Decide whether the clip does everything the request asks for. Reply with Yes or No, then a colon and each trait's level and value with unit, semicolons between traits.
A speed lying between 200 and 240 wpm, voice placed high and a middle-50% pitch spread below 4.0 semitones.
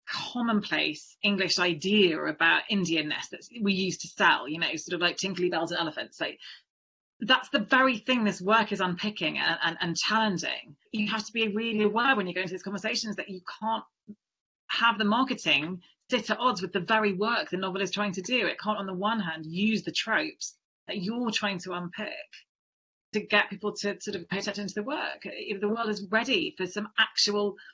Yes: fast, 205 wpm; high, 205 Hz; average, 3.1 semitones